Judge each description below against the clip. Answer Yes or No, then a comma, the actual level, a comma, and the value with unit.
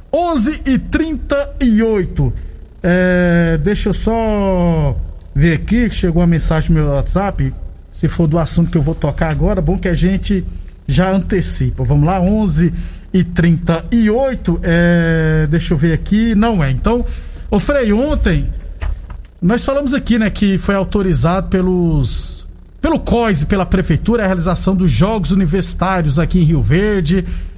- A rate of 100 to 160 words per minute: Yes, average, 150 wpm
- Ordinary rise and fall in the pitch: Yes, average, 4.5 semitones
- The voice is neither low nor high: Yes, medium, 180 Hz